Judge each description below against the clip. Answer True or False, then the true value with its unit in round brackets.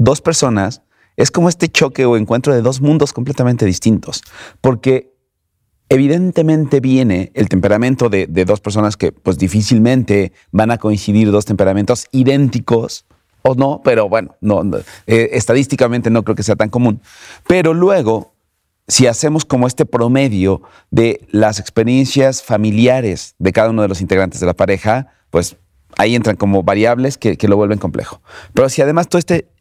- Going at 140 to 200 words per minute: True (160 wpm)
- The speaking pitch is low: True (115 Hz)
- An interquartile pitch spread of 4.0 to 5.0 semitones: True (4.3 semitones)